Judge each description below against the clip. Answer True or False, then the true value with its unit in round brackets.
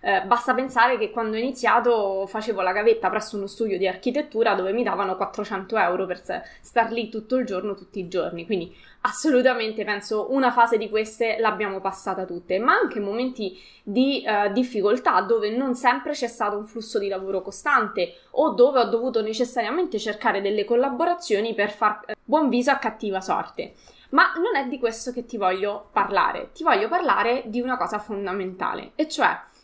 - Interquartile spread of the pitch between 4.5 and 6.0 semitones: False (3.5 semitones)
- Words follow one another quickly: True (180 wpm)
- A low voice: False (220 Hz)